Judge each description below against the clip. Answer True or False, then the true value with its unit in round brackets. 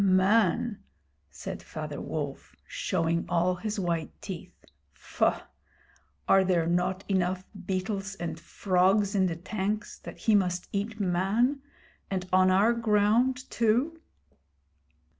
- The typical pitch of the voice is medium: False (195 Hz)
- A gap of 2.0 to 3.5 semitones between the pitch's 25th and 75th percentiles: True (2.9 semitones)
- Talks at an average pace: False (120 wpm)